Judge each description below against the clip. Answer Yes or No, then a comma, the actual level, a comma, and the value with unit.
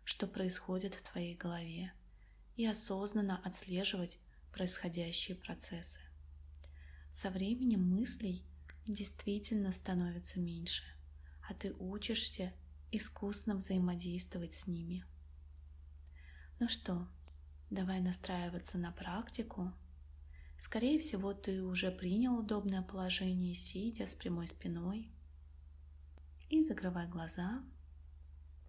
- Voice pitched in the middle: Yes, medium, 175 Hz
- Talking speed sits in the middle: No, slow, 90 wpm